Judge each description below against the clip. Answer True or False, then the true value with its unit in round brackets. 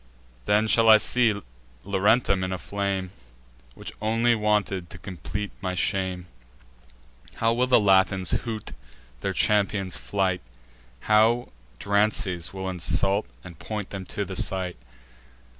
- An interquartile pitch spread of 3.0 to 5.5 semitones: False (2.4 semitones)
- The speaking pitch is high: False (100 Hz)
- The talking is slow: True (125 wpm)